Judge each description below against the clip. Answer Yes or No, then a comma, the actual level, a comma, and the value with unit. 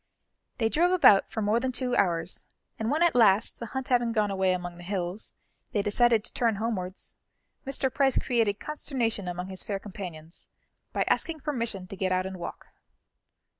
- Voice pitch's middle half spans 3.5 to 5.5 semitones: Yes, average, 4.7 semitones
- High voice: Yes, high, 215 Hz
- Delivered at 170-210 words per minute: Yes, average, 180 wpm